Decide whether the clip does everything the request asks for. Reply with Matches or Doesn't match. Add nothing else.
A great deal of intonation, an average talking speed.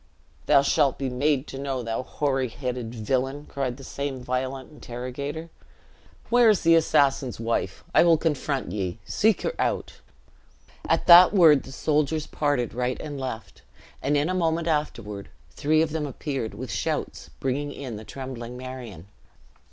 Doesn't match